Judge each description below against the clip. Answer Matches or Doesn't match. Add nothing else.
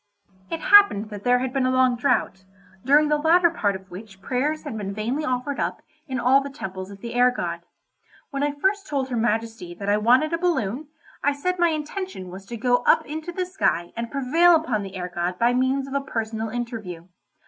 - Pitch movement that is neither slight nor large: Doesn't match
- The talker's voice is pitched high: Matches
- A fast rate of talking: Matches